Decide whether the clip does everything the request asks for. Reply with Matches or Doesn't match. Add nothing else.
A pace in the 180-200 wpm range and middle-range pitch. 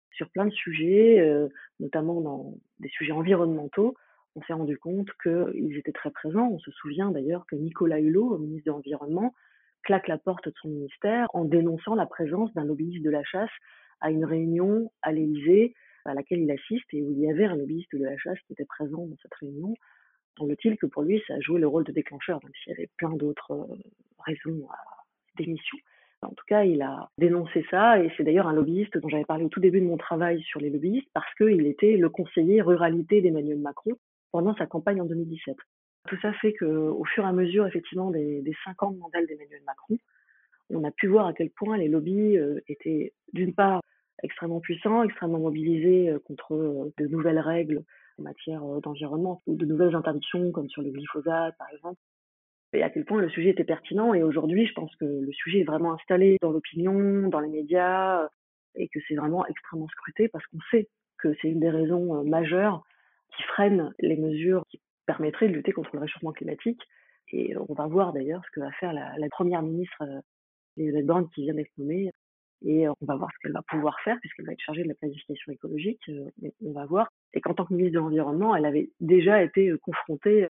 Doesn't match